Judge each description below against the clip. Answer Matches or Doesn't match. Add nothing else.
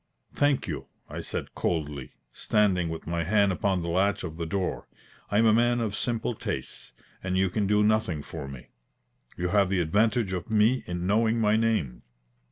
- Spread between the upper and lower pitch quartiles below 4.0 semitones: Doesn't match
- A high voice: Doesn't match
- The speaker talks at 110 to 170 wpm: Doesn't match